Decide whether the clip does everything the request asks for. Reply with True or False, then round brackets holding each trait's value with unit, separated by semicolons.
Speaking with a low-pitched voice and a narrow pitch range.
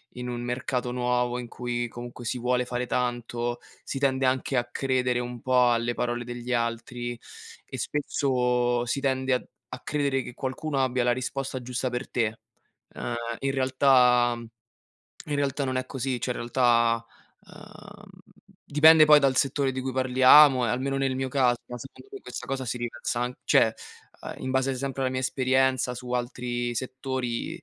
True (125 Hz; 1.5 semitones)